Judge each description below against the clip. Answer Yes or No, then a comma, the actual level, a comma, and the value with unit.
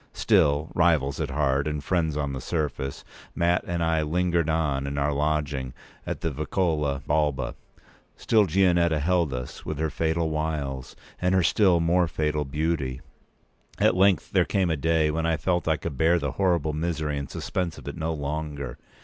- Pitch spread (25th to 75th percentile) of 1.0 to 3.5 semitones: Yes, average, 2.9 semitones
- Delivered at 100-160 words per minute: No, average, 175 wpm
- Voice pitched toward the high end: No, very low, 80 Hz